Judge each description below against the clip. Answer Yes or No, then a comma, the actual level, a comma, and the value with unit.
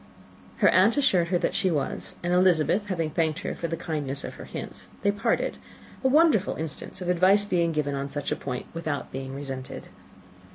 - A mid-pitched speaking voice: Yes, medium, 170 Hz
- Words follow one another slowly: No, average, 195 wpm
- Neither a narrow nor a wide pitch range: Yes, average, 4.7 semitones